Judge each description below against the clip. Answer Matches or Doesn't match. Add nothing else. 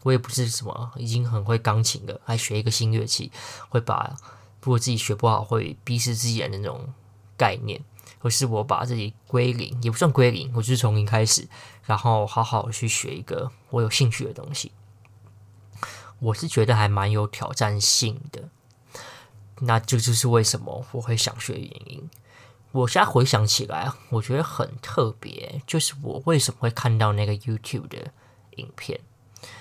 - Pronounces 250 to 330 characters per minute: Matches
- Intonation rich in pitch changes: Doesn't match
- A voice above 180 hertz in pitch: Doesn't match